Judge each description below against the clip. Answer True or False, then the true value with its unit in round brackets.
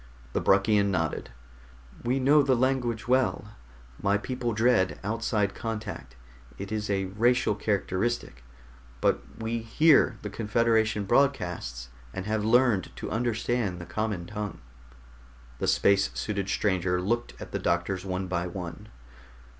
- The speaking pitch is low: True (105 Hz)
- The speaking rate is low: True (130 wpm)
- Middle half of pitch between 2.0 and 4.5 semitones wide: True (3.8 semitones)